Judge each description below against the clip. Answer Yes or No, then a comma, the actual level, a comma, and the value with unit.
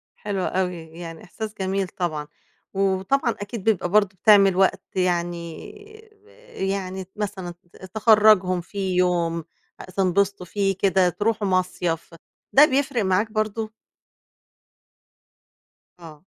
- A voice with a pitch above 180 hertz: Yes, high, 190 Hz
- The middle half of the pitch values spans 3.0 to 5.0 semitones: No, narrow, 2.5 semitones